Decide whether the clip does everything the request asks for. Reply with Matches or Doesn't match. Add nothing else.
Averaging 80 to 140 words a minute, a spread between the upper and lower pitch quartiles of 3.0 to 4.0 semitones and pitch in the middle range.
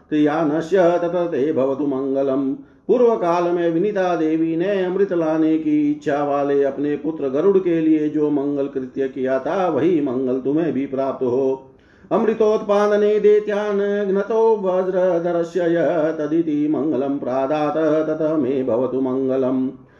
Doesn't match